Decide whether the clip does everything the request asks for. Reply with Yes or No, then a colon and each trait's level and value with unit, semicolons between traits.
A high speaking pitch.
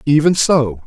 No: medium, 145 Hz